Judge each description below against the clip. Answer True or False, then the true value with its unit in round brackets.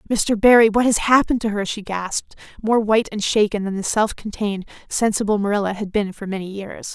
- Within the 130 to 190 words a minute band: False (200 wpm)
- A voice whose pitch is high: True (210 Hz)